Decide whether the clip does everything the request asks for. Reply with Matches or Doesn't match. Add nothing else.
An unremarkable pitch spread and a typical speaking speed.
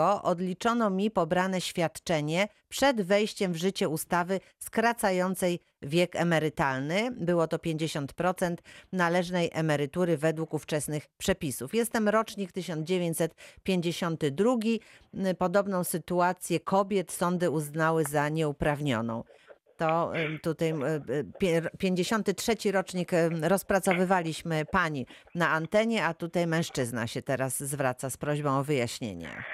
Doesn't match